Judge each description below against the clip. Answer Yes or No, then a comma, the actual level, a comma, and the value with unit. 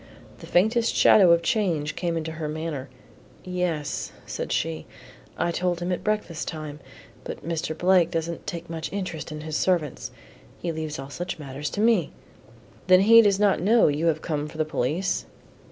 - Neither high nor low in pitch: Yes, medium, 165 Hz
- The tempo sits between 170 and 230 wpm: Yes, average, 180 wpm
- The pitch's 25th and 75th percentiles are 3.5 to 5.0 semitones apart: No, average, 3.0 semitones